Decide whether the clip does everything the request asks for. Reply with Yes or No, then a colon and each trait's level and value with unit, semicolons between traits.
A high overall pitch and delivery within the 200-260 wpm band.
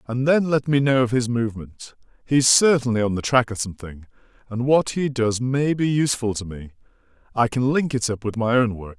No: low, 120 Hz; fast, 205 wpm